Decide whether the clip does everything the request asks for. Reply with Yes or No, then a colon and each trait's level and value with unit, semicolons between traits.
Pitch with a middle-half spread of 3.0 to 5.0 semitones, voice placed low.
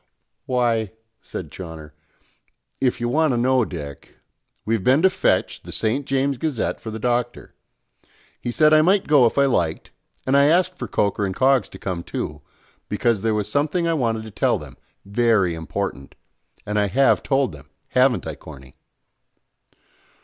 No: wide, 5.4 semitones; low, 120 Hz